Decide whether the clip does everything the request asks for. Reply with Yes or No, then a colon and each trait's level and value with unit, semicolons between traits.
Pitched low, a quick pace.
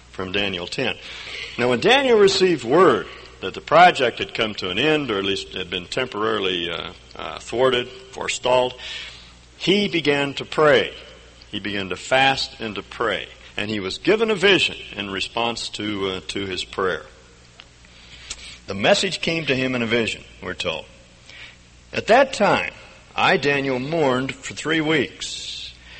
No: low, 110 Hz; average, 160 wpm